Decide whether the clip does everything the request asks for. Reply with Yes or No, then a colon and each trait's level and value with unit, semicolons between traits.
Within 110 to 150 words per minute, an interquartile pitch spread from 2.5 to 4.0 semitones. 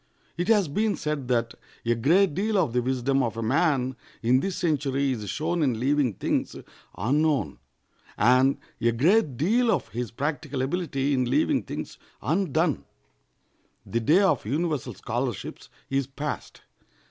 No: average, 145 wpm; average, 4.7 semitones